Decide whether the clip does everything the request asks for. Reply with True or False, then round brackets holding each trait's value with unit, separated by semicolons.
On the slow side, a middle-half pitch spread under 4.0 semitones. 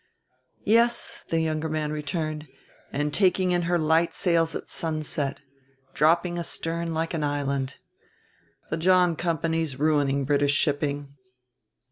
True (120 wpm; 2.5 semitones)